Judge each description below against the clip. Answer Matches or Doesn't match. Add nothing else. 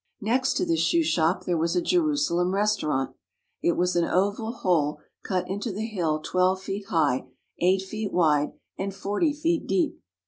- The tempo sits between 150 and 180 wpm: Matches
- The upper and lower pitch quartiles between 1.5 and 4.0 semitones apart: Doesn't match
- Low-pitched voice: Doesn't match